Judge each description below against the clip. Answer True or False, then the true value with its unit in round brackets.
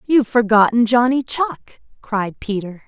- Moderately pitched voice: False (230 Hz)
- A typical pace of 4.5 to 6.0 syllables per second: False (4.3 syllables/s)